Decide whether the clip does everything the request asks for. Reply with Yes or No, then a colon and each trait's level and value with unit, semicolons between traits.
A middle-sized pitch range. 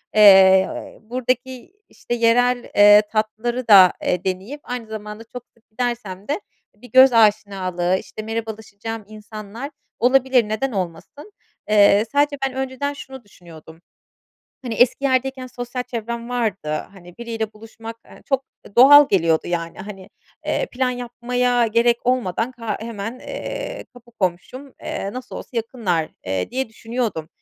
Yes: average, 3.7 semitones